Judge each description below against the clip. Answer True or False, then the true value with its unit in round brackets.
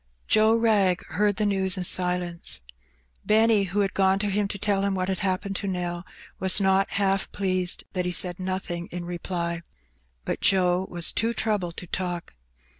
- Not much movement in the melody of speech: True (2.0 semitones)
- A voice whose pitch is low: False (190 Hz)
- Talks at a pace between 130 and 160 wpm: False (180 wpm)